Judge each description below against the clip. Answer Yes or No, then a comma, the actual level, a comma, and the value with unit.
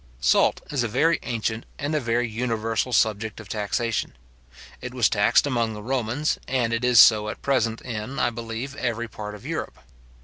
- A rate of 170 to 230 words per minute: Yes, average, 180 wpm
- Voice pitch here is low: Yes, low, 115 Hz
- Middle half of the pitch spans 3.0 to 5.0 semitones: No, narrow, 2.4 semitones